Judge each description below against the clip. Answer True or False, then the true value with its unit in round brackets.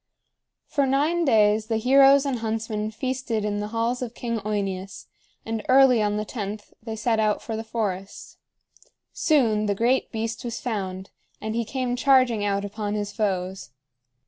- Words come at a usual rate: True (165 wpm)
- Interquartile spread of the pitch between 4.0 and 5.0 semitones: False (3.0 semitones)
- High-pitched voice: True (220 Hz)